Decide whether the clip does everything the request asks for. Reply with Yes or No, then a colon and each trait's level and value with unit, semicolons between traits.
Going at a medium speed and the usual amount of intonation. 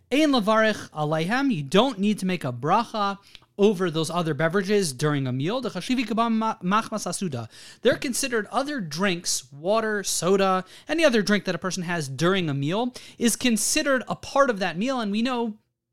Yes: average, 165 wpm; average, 5.0 semitones